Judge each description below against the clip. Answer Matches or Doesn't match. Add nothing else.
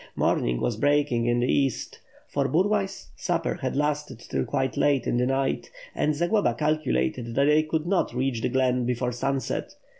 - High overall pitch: Doesn't match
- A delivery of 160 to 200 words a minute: Matches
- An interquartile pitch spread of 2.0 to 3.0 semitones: Doesn't match